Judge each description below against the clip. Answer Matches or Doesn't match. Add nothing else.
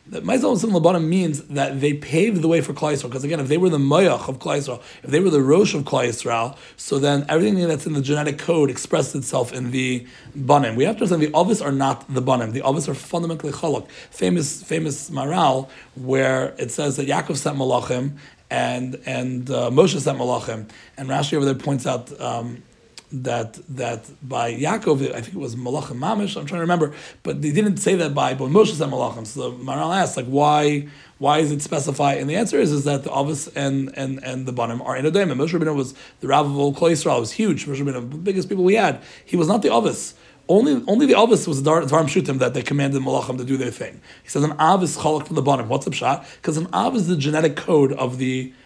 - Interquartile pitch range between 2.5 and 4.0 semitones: Matches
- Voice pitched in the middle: Matches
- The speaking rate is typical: Doesn't match